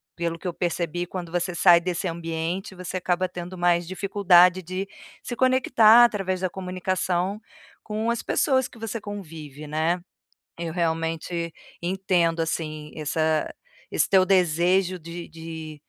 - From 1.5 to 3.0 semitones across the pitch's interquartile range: Yes, narrow, 2.4 semitones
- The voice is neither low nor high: Yes, medium, 175 Hz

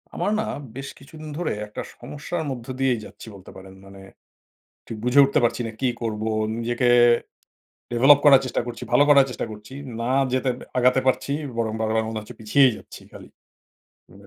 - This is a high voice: No, low, 125 Hz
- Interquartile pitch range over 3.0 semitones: Yes, average, 3.6 semitones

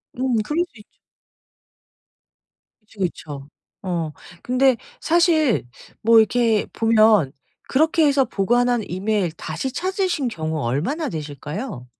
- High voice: Yes, high, 225 Hz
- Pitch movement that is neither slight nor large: No, wide, 7.6 semitones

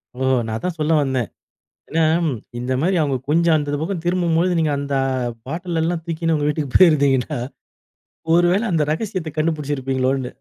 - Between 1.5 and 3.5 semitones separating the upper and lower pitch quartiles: Yes, average, 3.2 semitones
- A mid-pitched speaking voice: Yes, medium, 155 Hz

